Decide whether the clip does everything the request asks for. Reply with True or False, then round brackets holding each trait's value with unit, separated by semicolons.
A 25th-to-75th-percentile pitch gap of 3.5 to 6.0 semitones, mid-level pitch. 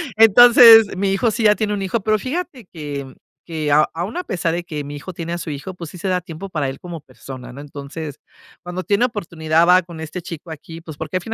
True (4.4 semitones; 175 Hz)